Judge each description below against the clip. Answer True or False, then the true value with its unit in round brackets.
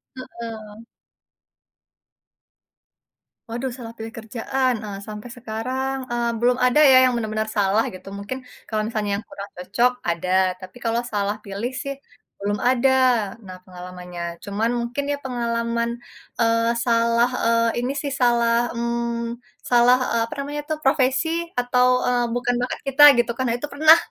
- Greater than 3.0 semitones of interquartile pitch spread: False (2.5 semitones)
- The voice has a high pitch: True (235 Hz)